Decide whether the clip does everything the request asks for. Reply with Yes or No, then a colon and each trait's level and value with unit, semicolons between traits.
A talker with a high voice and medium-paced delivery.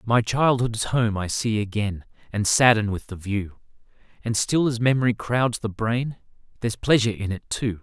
No: low, 110 Hz; average, 175 wpm